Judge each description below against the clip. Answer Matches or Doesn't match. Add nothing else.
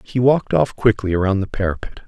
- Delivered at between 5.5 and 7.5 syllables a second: Matches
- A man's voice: Matches